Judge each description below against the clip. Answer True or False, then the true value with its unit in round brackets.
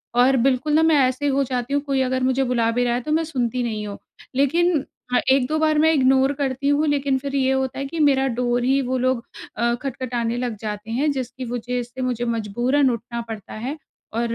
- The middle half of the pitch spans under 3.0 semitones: True (2.4 semitones)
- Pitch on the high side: True (260 Hz)